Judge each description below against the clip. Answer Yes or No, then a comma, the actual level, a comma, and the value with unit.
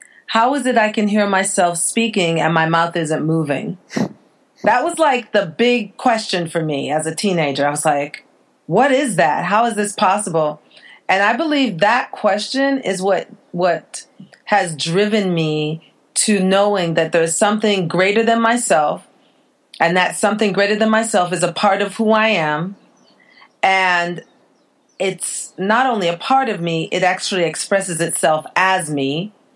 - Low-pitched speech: No, high, 195 Hz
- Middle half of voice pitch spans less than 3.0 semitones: No, average, 4.8 semitones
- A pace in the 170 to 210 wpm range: No, average, 160 wpm